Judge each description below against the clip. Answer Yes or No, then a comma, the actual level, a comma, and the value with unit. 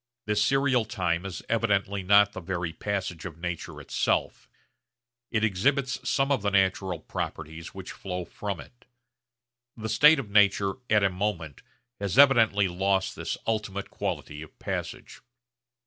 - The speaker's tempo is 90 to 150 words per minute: Yes, average, 145 wpm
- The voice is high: No, low, 100 Hz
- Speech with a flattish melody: No, average, 3.2 semitones